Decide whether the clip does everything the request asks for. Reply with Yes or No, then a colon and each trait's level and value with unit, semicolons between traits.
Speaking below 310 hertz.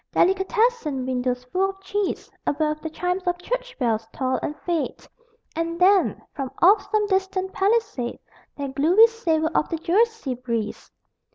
No: very high, 350 Hz